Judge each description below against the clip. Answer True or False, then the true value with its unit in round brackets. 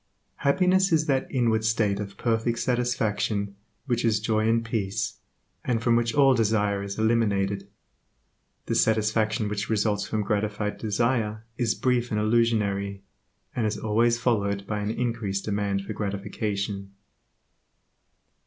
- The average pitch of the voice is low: True (110 Hz)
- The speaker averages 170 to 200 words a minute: False (135 wpm)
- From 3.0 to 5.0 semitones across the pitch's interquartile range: False (2.4 semitones)